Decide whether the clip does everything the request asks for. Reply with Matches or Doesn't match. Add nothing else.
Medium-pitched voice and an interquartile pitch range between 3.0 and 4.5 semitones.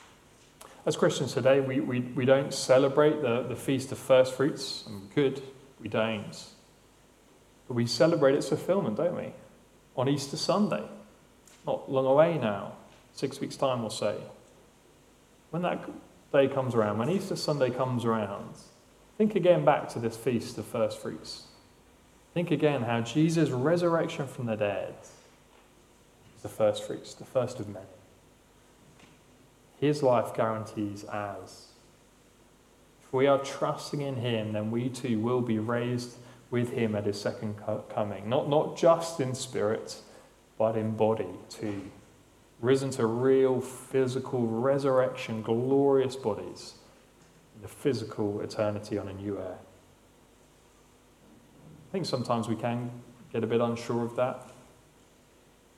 Doesn't match